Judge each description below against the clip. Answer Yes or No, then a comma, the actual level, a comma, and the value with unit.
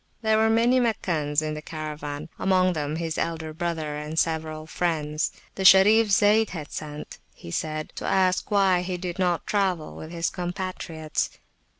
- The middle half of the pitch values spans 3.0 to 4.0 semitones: Yes, average, 3.5 semitones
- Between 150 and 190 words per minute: Yes, average, 165 wpm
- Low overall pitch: No, medium, 170 Hz